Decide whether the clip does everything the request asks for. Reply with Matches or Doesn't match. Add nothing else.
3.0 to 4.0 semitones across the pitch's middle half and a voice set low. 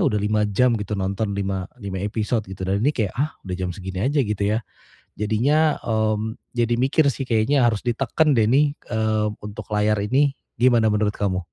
Matches